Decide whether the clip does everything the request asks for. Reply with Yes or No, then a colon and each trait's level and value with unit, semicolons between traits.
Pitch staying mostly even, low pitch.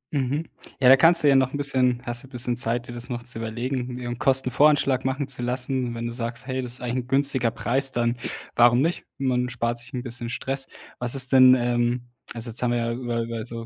Yes: narrow, 1.8 semitones; low, 125 Hz